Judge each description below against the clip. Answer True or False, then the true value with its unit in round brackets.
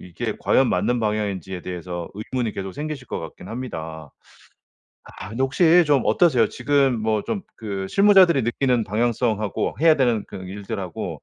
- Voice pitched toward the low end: True (115 Hz)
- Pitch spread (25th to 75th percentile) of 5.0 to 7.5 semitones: True (5.5 semitones)